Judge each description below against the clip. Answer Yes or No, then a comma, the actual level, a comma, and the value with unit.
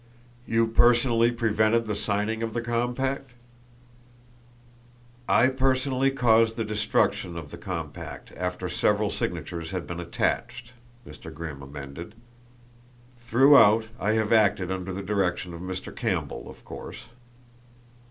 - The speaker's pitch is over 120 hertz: No, low, 110 Hz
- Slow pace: Yes, slow, 125 wpm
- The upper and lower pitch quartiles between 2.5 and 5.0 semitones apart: Yes, average, 4.5 semitones